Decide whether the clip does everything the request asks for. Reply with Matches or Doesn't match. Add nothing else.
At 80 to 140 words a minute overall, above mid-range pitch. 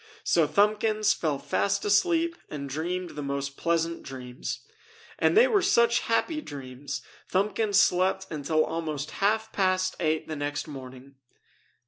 Doesn't match